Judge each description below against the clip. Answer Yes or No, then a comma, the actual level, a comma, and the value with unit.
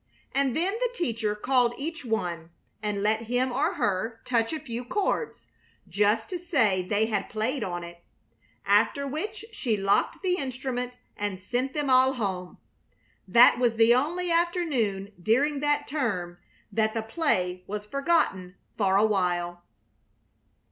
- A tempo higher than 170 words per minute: No, average, 150 wpm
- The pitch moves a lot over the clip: Yes, wide, 5.7 semitones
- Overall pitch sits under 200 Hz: No, high, 230 Hz